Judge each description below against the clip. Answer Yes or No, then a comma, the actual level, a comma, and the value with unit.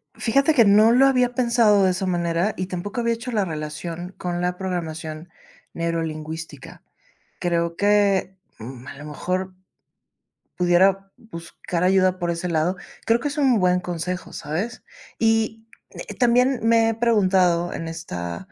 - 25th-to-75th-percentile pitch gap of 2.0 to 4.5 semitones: No, average, 4.9 semitones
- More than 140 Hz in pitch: Yes, medium, 185 Hz